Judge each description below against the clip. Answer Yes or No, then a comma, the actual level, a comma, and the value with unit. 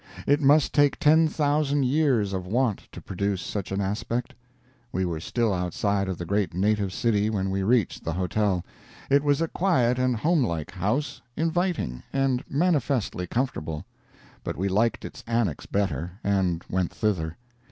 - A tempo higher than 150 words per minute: Yes, average, 160 wpm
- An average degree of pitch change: No, wide, 6.5 semitones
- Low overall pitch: Yes, low, 105 Hz